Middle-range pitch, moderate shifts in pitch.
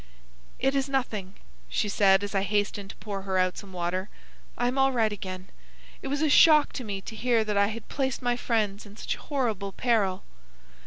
No: high, 210 Hz; average, 4.2 semitones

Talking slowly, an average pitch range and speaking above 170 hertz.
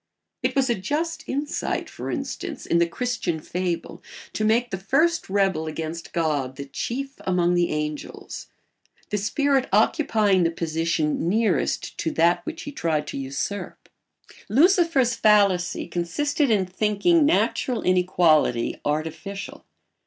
No: slow, 130 wpm; wide, 7.4 semitones; high, 190 Hz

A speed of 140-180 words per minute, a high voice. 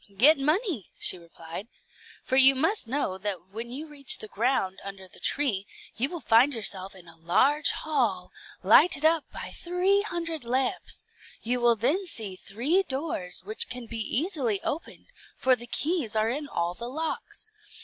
Yes: average, 170 wpm; very high, 250 Hz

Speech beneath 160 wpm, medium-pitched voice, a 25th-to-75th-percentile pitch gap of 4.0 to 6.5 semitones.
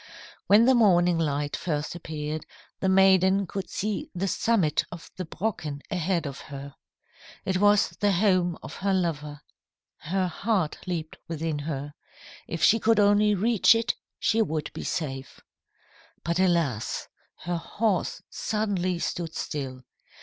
Yes: average, 140 wpm; medium, 175 Hz; average, 4.5 semitones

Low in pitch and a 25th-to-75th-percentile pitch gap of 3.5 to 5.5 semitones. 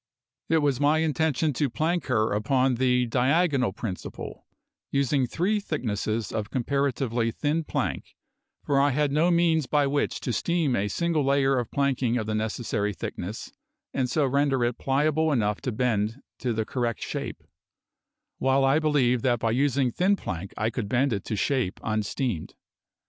Yes: low, 130 Hz; average, 4.3 semitones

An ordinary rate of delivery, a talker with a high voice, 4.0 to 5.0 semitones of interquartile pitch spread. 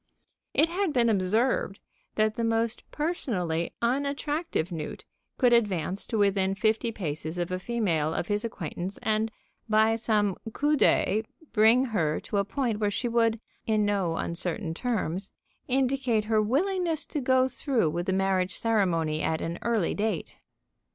Yes: average, 150 wpm; high, 215 Hz; average, 4.6 semitones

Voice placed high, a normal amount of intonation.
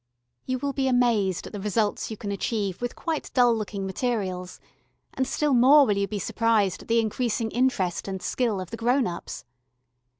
Yes: high, 225 Hz; average, 3.9 semitones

